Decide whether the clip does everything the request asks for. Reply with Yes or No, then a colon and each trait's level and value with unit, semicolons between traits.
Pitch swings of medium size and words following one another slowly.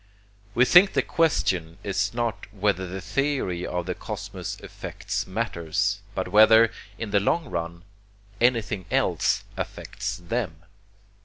Yes: average, 4.4 semitones; slow, 130 wpm